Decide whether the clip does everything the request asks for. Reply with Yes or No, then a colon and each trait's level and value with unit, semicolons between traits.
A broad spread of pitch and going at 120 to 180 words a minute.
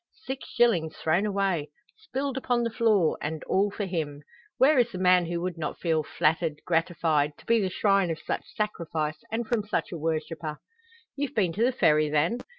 No: wide, 6.0 semitones; average, 190 wpm